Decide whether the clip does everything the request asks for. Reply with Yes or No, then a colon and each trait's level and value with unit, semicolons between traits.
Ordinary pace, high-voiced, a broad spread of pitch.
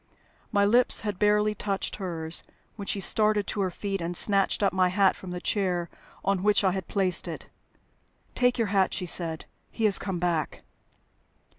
No: average, 180 wpm; high, 195 Hz; narrow, 2.5 semitones